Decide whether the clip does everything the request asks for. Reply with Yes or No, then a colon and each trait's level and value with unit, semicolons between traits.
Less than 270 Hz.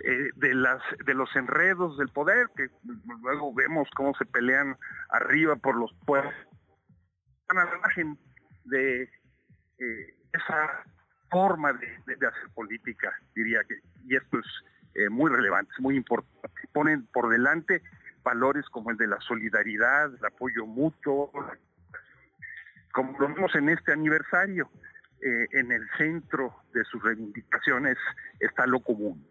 Yes: low, 135 Hz